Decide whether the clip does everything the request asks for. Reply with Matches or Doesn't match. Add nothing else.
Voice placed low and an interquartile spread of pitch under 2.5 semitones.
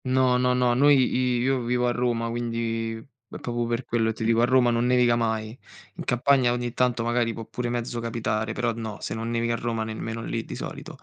Matches